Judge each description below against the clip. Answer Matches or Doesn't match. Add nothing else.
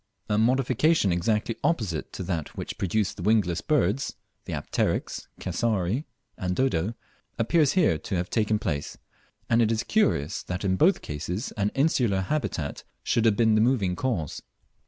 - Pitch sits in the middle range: Doesn't match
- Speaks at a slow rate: Doesn't match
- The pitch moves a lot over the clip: Matches